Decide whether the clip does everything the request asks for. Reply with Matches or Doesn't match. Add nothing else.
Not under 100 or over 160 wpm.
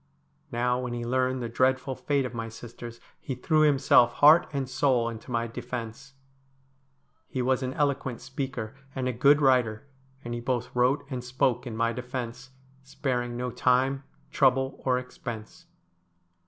Matches